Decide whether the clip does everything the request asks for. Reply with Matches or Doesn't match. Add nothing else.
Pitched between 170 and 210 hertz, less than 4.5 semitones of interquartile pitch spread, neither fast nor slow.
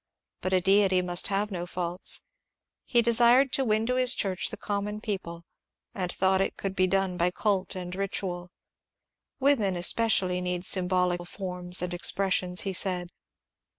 Matches